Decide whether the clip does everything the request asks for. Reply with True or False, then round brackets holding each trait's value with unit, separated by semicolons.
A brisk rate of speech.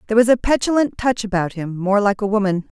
True (215 wpm)